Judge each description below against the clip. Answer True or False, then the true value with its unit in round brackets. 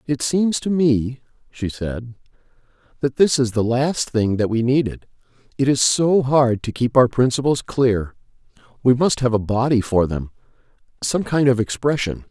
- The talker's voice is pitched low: True (125 Hz)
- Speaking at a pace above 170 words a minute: False (160 wpm)